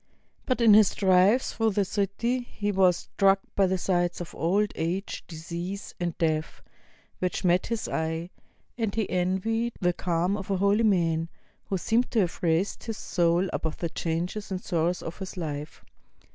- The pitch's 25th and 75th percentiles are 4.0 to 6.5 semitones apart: No, average, 3.2 semitones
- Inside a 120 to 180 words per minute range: Yes, average, 170 wpm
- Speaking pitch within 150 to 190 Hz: Yes, medium, 185 Hz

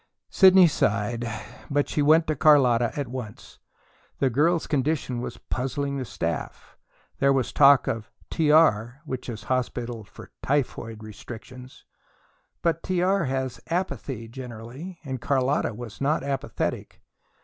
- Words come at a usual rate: No, slow, 125 wpm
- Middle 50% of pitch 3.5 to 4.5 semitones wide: Yes, average, 4.0 semitones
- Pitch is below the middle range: Yes, low, 130 Hz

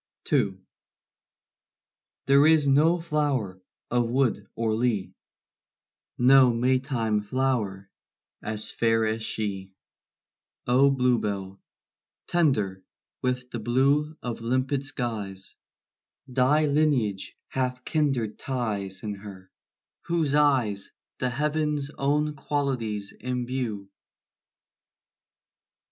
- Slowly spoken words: Yes, slow, 90 wpm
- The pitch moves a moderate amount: Yes, average, 4.7 semitones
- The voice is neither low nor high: No, low, 125 Hz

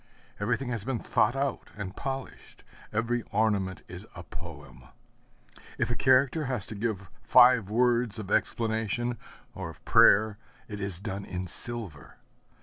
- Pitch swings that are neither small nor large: Yes, average, 3.4 semitones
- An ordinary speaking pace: Yes, average, 145 wpm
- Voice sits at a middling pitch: No, low, 110 Hz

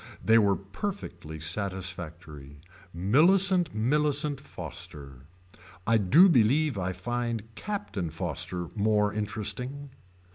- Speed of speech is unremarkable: No, slow, 95 wpm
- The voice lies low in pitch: Yes, low, 105 Hz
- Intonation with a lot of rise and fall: Yes, wide, 7.9 semitones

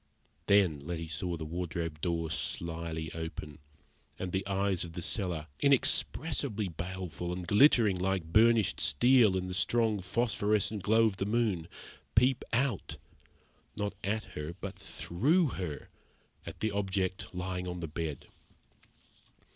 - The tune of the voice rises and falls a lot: No, average, 4.2 semitones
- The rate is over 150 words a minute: No, slow, 135 wpm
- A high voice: No, very low, 95 Hz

